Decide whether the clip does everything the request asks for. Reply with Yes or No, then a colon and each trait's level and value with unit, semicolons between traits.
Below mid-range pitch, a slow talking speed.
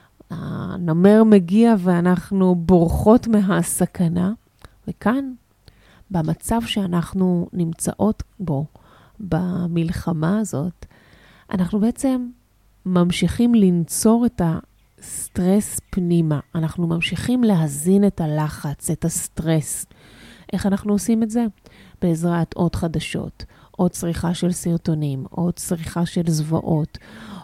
No: medium, 180 Hz; slow, 90 wpm